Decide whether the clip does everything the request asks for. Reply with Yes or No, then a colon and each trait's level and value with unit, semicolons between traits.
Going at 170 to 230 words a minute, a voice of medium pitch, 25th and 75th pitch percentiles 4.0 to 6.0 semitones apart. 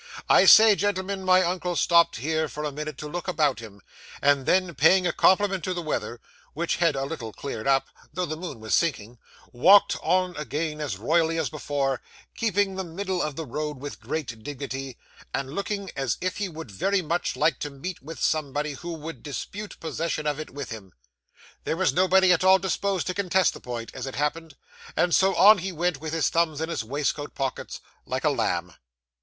Yes: average, 200 wpm; medium, 160 Hz; average, 4.5 semitones